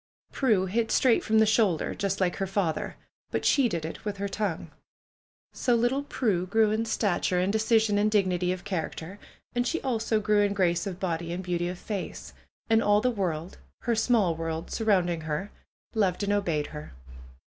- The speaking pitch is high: Yes, high, 200 Hz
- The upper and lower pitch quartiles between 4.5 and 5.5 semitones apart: No, average, 3.8 semitones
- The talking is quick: No, average, 190 wpm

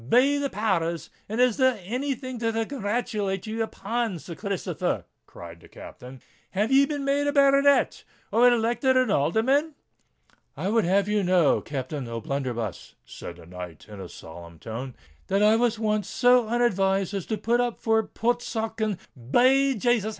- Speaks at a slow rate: No, average, 165 wpm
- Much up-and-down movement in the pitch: Yes, wide, 6.4 semitones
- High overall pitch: Yes, high, 220 Hz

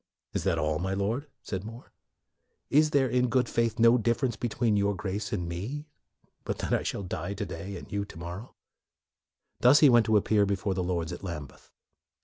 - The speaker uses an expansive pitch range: No, average, 4.1 semitones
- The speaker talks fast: Yes, fast, 220 wpm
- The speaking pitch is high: No, low, 105 Hz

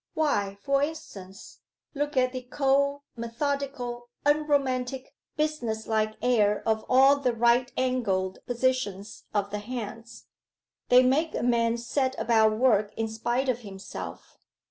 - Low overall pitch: No, high, 245 Hz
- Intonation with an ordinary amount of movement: Yes, average, 3.6 semitones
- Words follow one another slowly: Yes, slow, 130 wpm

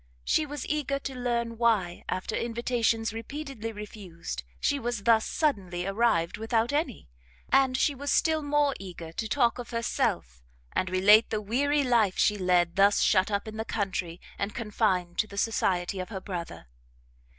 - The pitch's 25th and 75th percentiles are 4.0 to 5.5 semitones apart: Yes, average, 4.6 semitones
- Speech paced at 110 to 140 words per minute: No, average, 165 wpm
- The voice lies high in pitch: Yes, high, 220 Hz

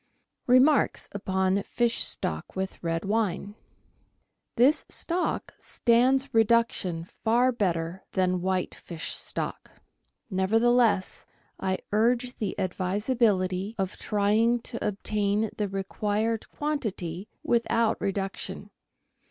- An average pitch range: Yes, average, 3.7 semitones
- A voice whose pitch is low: No, high, 210 Hz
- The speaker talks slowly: Yes, slow, 100 wpm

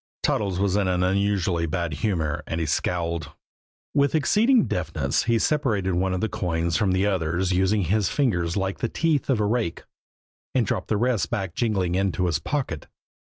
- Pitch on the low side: Yes, very low, 95 Hz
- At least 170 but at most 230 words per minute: Yes, average, 180 wpm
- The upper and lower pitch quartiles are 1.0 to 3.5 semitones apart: No, average, 4.3 semitones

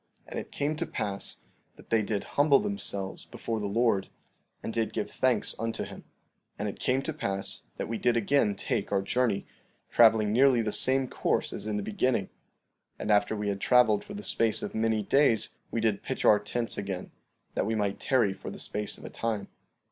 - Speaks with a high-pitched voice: No, low, 110 Hz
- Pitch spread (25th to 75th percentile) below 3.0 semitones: No, average, 3.3 semitones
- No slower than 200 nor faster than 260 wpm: Yes, fast, 205 wpm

